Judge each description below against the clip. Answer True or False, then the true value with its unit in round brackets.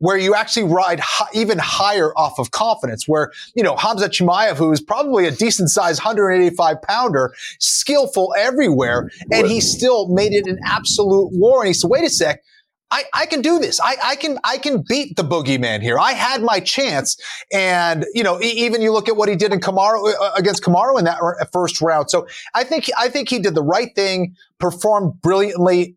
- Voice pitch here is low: False (200 Hz)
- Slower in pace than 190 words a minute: False (205 wpm)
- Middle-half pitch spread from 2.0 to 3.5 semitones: False (4.4 semitones)